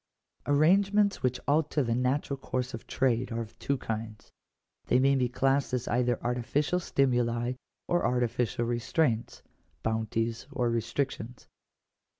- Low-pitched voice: Yes, low, 125 Hz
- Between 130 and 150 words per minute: Yes, average, 140 wpm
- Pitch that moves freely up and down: No, average, 2.9 semitones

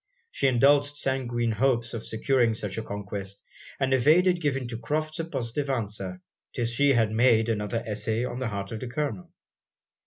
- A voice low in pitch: Yes, low, 120 Hz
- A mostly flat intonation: No, average, 3.7 semitones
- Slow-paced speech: No, average, 175 wpm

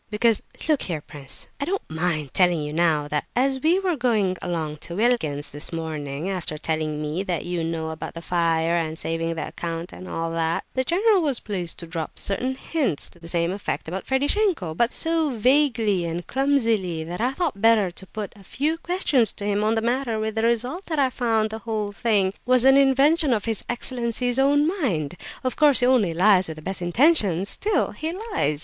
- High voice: Yes, high, 210 Hz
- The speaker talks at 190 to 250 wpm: Yes, fast, 205 wpm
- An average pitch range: No, wide, 7.8 semitones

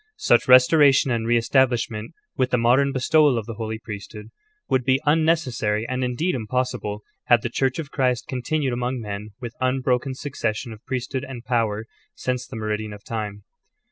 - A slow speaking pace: No, average, 170 wpm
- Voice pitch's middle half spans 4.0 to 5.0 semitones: No, average, 2.9 semitones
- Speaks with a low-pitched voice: Yes, low, 125 Hz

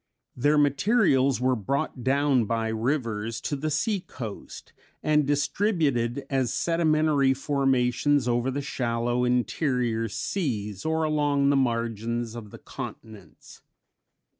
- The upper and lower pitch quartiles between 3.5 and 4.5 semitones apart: Yes, average, 3.8 semitones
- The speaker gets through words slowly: Yes, slow, 115 wpm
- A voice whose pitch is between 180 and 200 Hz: No, low, 130 Hz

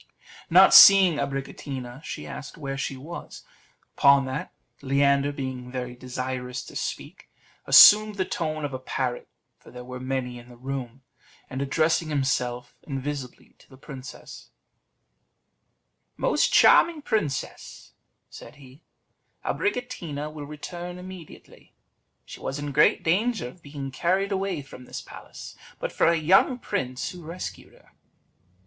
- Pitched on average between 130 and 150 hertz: Yes, medium, 140 Hz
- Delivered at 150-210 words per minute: No, slow, 135 wpm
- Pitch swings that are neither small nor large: Yes, average, 4.5 semitones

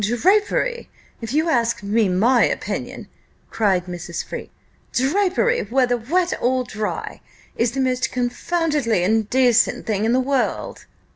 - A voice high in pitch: Yes, high, 245 Hz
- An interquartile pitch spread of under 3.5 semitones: No, average, 4.3 semitones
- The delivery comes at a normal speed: No, slow, 130 wpm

